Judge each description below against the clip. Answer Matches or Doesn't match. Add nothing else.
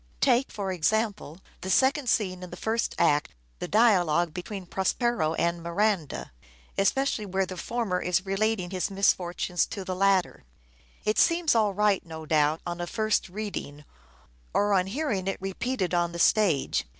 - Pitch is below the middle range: Doesn't match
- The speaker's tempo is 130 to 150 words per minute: Doesn't match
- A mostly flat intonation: Doesn't match